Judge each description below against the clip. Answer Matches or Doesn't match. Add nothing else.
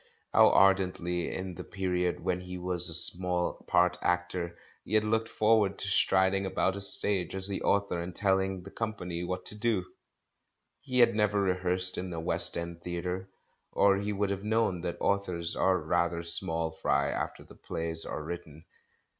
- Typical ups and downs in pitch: Doesn't match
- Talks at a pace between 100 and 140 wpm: Doesn't match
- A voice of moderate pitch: Doesn't match